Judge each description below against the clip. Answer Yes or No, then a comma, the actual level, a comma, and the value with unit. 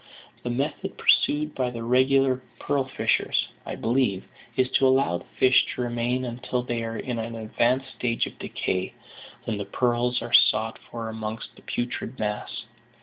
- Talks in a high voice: No, low, 120 Hz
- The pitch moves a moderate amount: No, narrow, 2.2 semitones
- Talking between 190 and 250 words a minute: No, average, 165 wpm